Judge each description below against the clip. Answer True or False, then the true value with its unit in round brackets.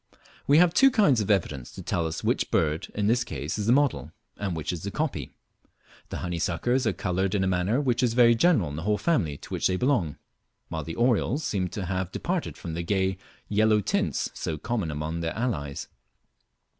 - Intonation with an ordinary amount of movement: False (6.4 semitones)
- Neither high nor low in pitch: False (100 Hz)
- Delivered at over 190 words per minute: True (205 wpm)